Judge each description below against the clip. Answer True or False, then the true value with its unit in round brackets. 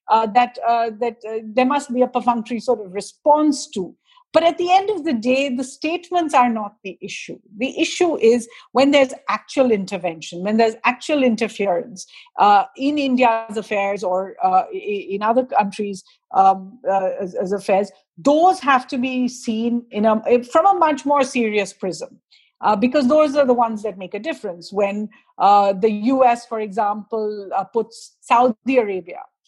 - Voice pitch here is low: False (235 Hz)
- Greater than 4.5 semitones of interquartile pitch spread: True (5.2 semitones)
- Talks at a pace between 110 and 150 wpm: False (175 wpm)